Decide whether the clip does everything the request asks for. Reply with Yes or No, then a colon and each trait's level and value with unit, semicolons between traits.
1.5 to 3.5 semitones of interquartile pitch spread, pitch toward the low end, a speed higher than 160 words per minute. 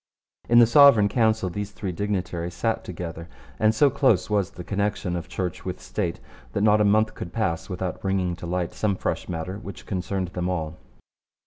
Yes: average, 3.2 semitones; very low, 95 Hz; average, 190 wpm